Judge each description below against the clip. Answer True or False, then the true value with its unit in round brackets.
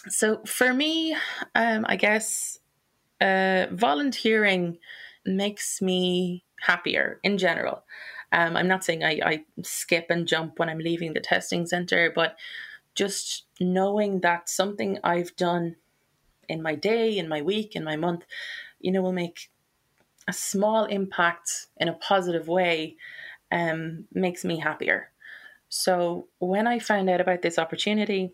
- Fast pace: False (140 wpm)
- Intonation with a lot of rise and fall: False (3.8 semitones)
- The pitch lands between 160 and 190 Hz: True (185 Hz)